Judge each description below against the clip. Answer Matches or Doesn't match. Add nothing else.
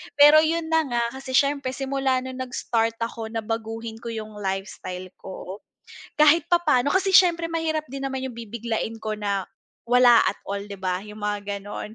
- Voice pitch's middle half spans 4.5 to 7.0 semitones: Matches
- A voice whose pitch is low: Doesn't match